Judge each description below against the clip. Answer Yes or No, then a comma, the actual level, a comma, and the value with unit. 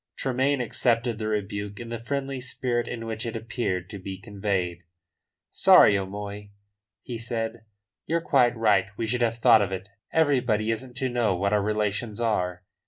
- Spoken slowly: No, average, 170 wpm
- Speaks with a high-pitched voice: No, low, 115 Hz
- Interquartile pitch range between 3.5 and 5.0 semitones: No, average, 3.1 semitones